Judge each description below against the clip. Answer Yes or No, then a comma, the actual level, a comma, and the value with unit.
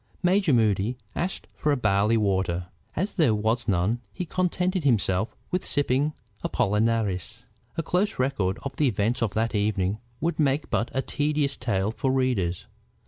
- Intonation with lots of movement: Yes, wide, 6.3 semitones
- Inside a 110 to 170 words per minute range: Yes, average, 150 wpm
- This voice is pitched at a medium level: No, low, 115 Hz